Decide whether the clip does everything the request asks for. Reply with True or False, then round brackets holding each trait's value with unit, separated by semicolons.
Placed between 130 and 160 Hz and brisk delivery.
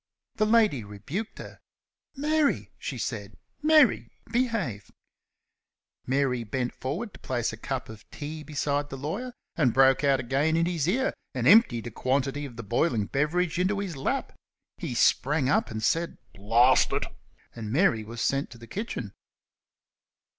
False (140 Hz; 155 wpm)